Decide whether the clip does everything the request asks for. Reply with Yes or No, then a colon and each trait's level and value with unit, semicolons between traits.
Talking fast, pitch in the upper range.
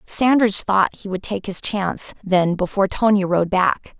No: average, 180 wpm; high, 195 Hz